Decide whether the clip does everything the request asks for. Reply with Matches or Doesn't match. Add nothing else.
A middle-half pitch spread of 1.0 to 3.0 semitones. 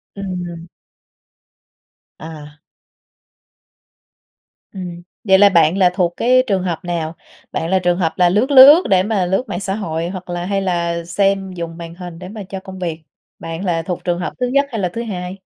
Matches